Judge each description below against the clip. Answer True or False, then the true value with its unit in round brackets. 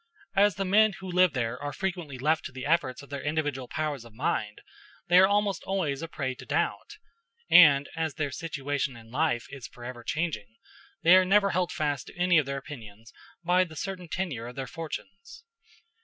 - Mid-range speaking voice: True (155 Hz)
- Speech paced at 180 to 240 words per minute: True (195 wpm)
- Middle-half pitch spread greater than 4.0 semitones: True (5.5 semitones)